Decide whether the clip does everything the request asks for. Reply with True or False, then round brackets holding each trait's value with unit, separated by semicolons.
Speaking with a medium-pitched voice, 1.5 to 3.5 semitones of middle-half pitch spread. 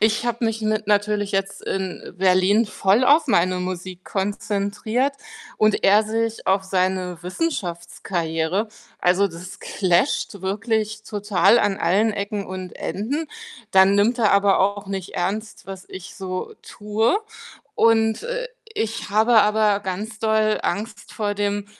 False (205 Hz; 2.4 semitones)